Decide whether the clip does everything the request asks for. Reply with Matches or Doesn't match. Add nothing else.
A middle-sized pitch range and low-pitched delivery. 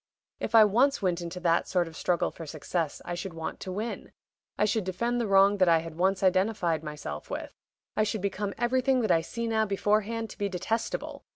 Doesn't match